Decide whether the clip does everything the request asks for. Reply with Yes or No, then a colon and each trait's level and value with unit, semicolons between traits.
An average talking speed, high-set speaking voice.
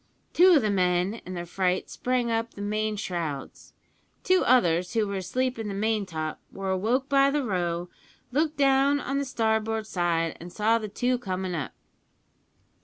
Yes: average, 180 wpm; high, 215 Hz